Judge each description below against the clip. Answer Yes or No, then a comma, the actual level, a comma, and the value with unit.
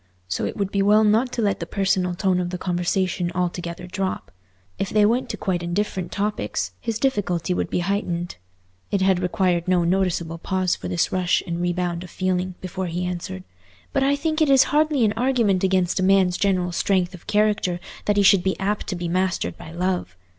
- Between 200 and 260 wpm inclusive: Yes, fast, 205 wpm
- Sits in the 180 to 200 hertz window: Yes, medium, 185 Hz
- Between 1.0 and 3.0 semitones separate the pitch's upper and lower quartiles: Yes, narrow, 2.6 semitones